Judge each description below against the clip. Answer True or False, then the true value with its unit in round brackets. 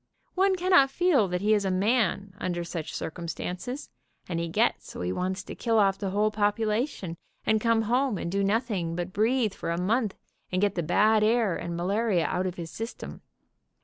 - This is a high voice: True (205 Hz)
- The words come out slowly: False (200 wpm)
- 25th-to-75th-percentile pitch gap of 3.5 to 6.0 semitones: True (4.1 semitones)